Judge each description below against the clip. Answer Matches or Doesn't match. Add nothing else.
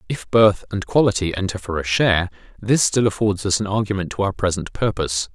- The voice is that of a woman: Doesn't match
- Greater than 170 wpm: Matches